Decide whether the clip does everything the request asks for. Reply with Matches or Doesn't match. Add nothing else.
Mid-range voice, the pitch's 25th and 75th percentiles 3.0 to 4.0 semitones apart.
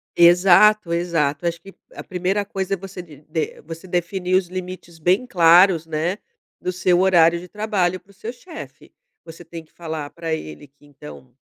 Doesn't match